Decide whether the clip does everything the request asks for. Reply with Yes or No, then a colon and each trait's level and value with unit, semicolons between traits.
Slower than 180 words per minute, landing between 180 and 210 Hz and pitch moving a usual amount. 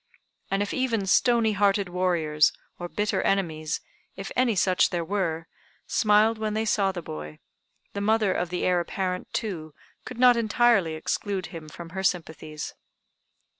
Yes: average, 155 wpm; high, 190 Hz; average, 4.1 semitones